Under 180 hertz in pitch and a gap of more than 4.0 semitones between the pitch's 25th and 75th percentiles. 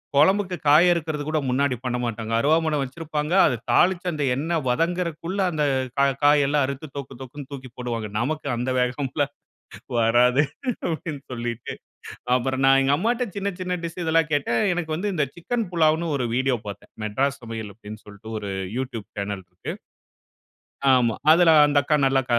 Yes: medium, 140 Hz; average, 4.7 semitones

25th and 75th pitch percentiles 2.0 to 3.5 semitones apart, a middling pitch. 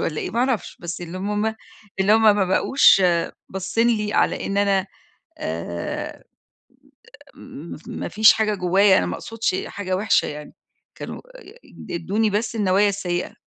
No: average, 3.1 semitones; high, 200 Hz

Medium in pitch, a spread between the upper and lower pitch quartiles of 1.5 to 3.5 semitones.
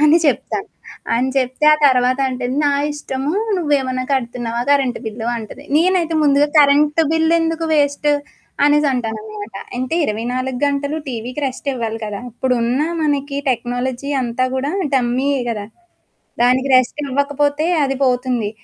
No: very high, 260 Hz; average, 2.9 semitones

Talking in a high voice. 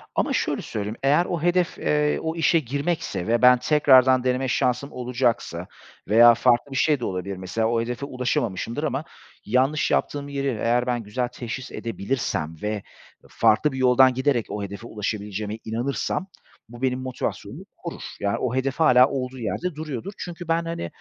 No: low, 125 Hz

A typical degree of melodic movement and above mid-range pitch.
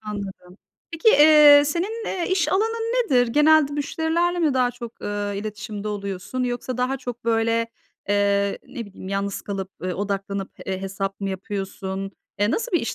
No: wide, 6.7 semitones; high, 225 Hz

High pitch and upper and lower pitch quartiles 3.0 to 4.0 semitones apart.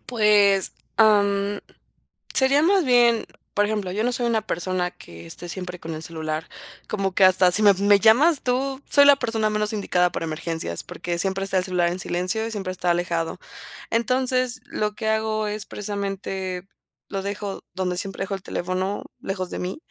Yes: high, 200 Hz; average, 3.3 semitones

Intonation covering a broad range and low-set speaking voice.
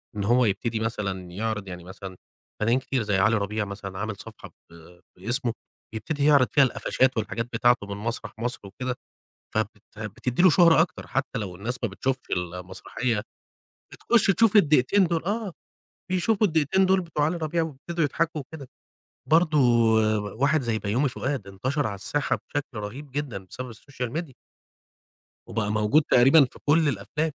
Yes: wide, 6.6 semitones; low, 125 Hz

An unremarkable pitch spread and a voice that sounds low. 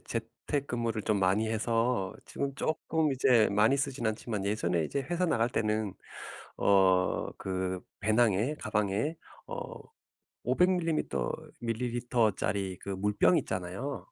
Yes: average, 4.8 semitones; low, 110 Hz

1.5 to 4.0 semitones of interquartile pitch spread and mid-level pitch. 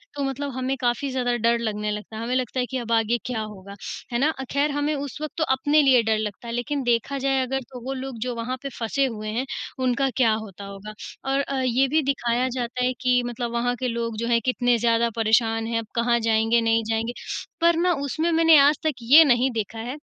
No: average, 2.9 semitones; high, 245 Hz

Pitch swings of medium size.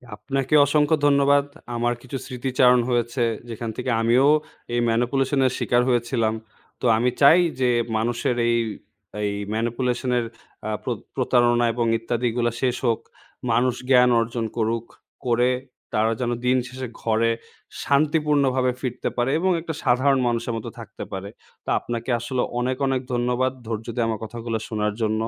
No: narrow, 2.0 semitones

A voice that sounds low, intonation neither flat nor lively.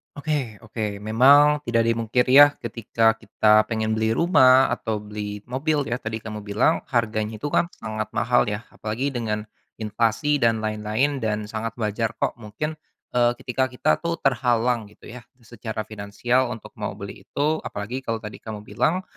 Yes: low, 115 Hz; average, 3.0 semitones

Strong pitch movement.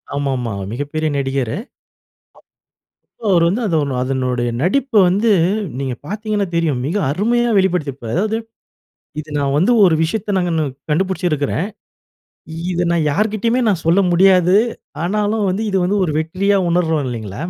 Yes: wide, 5.9 semitones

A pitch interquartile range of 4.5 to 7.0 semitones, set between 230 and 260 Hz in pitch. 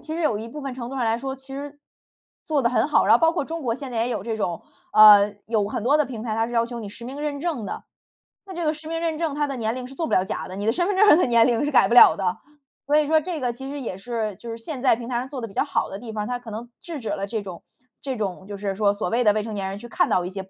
Yes: average, 5.0 semitones; high, 240 Hz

